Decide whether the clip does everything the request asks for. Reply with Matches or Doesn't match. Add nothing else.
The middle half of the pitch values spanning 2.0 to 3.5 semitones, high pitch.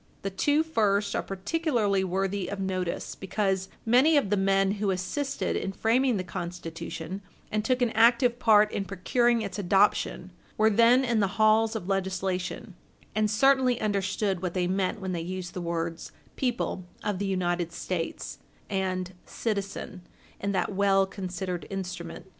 Matches